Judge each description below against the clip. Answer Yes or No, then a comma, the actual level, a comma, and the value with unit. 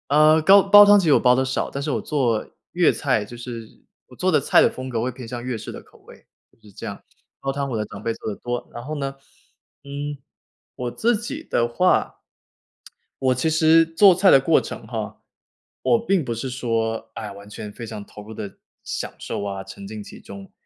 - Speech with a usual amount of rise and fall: No, wide, 5.7 semitones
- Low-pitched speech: Yes, low, 130 Hz